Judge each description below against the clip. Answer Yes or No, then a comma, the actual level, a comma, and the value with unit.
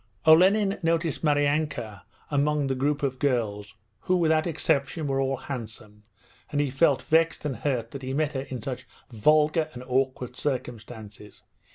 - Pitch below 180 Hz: Yes, medium, 140 Hz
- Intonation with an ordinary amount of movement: Yes, average, 3.7 semitones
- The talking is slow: No, average, 155 wpm